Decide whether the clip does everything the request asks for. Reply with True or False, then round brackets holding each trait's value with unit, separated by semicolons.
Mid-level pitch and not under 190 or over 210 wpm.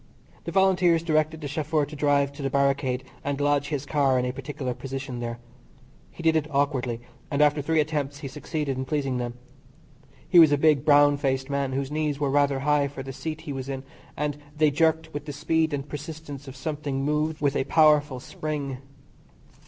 True (145 Hz; 200 wpm)